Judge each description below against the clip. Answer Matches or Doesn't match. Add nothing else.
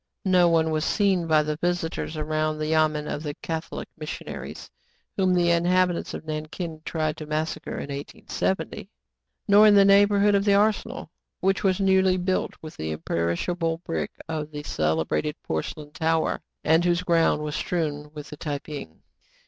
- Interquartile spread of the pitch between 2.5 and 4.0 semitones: Matches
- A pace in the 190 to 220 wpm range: Doesn't match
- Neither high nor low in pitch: Matches